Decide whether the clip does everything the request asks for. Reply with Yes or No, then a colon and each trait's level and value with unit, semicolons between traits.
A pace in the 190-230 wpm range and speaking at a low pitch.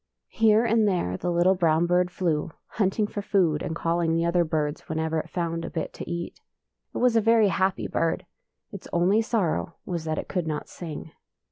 No: average, 200 wpm; medium, 175 Hz